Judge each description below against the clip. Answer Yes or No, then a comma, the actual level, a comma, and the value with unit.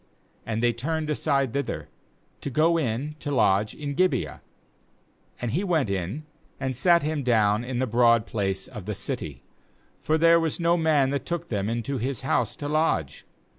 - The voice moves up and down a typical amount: No, wide, 5.8 semitones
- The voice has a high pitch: No, low, 135 Hz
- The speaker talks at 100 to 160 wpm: No, average, 170 wpm